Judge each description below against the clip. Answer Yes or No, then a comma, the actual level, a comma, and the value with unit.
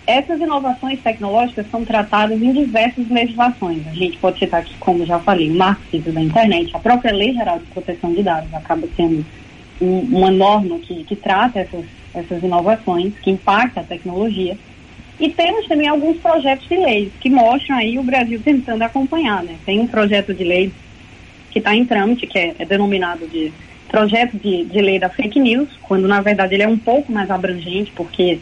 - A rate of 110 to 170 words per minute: No, fast, 185 wpm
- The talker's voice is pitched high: Yes, high, 205 Hz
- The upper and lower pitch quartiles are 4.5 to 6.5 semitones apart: Yes, average, 5.0 semitones